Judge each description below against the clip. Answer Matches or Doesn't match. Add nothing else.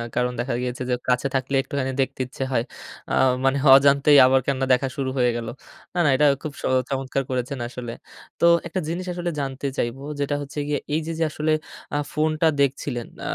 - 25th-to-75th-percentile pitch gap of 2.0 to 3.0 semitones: Matches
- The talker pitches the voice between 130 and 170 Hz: Matches